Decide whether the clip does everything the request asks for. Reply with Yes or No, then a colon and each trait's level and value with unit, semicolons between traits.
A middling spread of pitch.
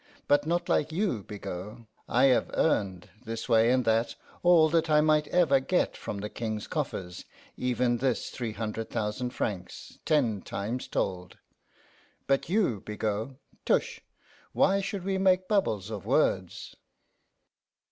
No: wide, 6.8 semitones